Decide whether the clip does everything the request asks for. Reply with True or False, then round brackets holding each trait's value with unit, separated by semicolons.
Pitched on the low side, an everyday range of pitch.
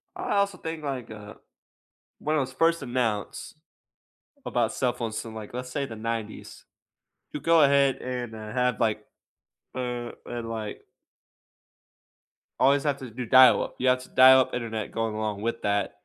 True (125 Hz; 3.0 semitones)